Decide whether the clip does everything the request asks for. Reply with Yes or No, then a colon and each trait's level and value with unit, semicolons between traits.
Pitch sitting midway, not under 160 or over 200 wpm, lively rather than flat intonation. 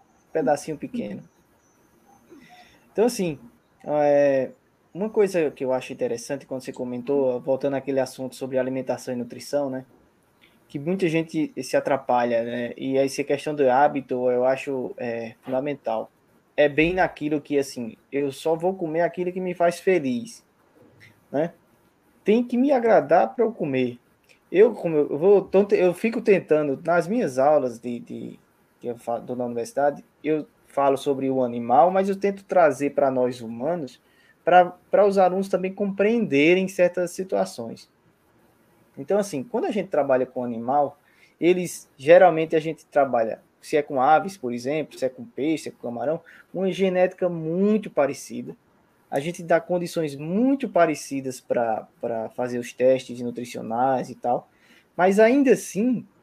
No: medium, 150 Hz; average, 150 wpm; wide, 5.9 semitones